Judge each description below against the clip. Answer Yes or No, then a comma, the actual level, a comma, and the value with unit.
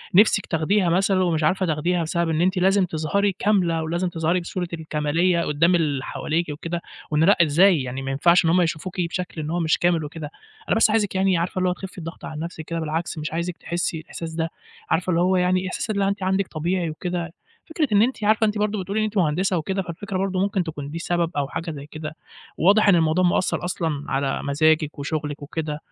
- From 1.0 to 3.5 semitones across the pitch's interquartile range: Yes, average, 3.0 semitones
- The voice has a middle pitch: Yes, medium, 170 Hz